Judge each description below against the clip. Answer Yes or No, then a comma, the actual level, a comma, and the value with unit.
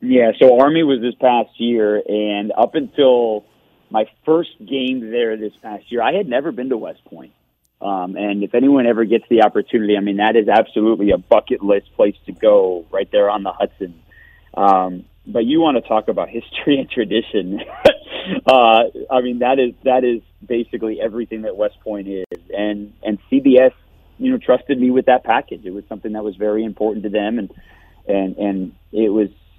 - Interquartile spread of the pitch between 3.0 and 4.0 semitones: Yes, average, 3.6 semitones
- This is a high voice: No, low, 115 Hz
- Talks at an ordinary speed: Yes, average, 195 wpm